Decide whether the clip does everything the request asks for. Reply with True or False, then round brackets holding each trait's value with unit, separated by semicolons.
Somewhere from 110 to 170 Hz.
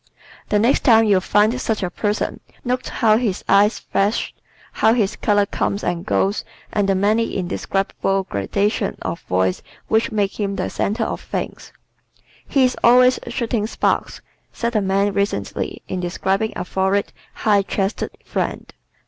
False (205 Hz)